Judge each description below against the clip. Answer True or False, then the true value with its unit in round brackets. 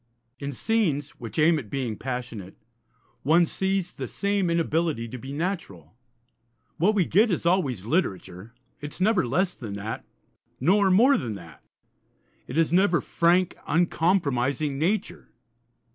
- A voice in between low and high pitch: True (155 Hz)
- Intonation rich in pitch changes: True (7.1 semitones)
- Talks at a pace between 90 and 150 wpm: True (140 wpm)